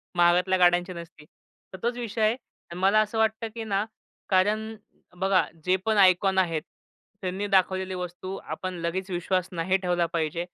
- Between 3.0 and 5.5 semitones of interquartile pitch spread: No, narrow, 2.6 semitones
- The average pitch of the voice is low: No, medium, 185 Hz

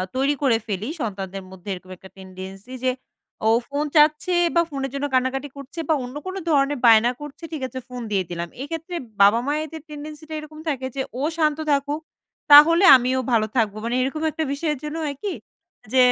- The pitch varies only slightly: No, average, 4.7 semitones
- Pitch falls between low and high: No, very high, 275 Hz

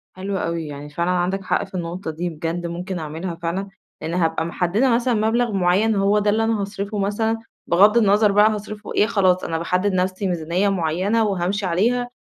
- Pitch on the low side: No, high, 190 Hz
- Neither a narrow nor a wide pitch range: Yes, average, 3.4 semitones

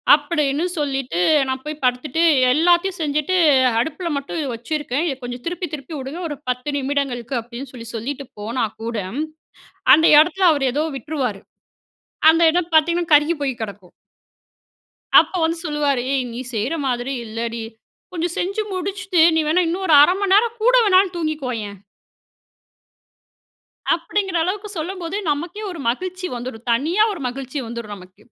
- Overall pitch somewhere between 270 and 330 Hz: Yes, very high, 295 Hz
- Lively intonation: Yes, wide, 5.7 semitones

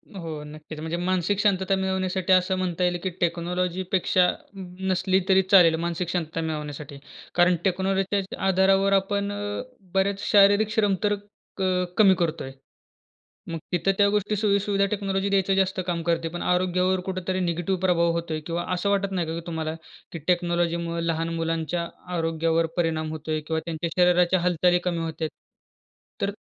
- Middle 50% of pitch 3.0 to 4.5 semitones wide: No, narrow, 2.4 semitones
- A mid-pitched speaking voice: Yes, medium, 180 Hz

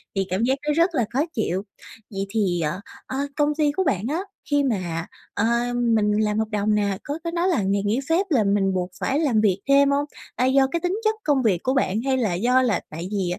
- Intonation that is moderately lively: No, wide, 6.2 semitones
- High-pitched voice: Yes, high, 230 Hz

